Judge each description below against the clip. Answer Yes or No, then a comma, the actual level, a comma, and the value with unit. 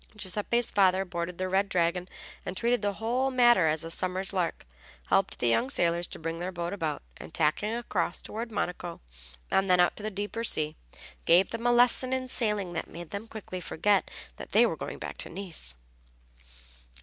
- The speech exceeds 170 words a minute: Yes, average, 190 wpm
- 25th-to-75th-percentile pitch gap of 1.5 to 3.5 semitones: No, average, 4.4 semitones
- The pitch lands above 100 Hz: Yes, high, 190 Hz